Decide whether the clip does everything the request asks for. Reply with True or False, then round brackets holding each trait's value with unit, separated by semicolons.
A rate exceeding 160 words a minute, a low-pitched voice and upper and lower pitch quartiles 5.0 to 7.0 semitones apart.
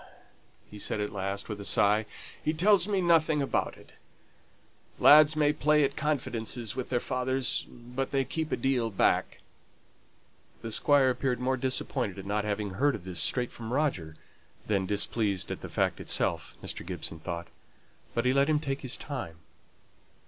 True (170 wpm; 125 Hz; 5.6 semitones)